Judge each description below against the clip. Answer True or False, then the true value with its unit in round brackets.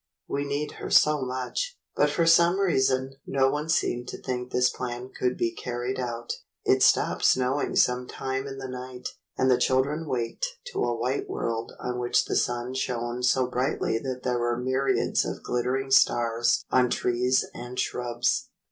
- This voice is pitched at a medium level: False (125 Hz)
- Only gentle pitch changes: True (1.6 semitones)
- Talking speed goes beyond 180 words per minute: False (175 wpm)